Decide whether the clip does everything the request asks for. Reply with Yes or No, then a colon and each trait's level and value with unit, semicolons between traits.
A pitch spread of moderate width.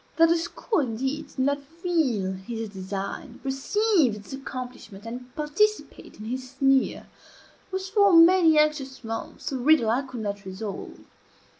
No: wide, 6.3 semitones